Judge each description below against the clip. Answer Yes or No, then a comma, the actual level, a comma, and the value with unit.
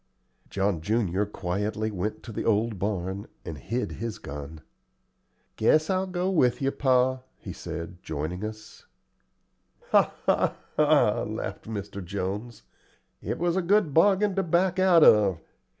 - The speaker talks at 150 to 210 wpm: No, average, 140 wpm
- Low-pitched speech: Yes, low, 110 Hz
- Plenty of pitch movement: Yes, wide, 8.5 semitones